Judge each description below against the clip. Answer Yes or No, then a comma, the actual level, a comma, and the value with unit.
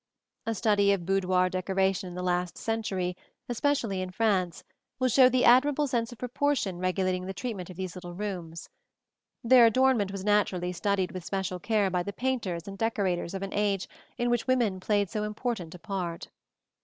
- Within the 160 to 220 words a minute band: Yes, average, 190 wpm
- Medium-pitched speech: No, high, 195 Hz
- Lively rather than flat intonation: No, average, 3.8 semitones